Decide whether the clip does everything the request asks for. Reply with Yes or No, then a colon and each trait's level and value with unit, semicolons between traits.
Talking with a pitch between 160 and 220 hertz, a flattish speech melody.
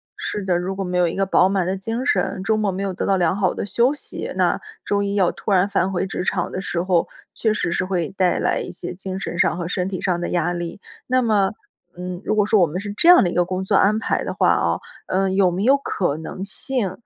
Yes: high, 190 Hz; narrow, 2.2 semitones